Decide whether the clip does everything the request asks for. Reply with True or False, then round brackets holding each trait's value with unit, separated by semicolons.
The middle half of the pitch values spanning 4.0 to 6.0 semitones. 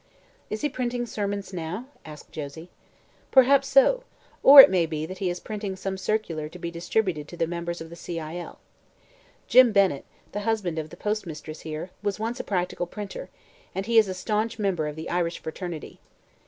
True (4.5 semitones)